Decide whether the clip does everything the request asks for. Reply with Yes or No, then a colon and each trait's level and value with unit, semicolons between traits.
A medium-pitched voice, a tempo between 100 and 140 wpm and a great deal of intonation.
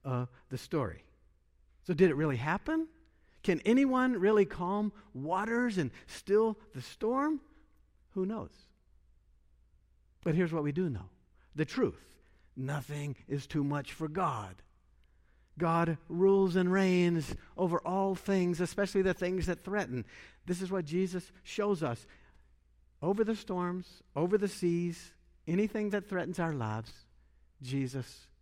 Yes: medium, 170 Hz; slow, 135 wpm; wide, 7.5 semitones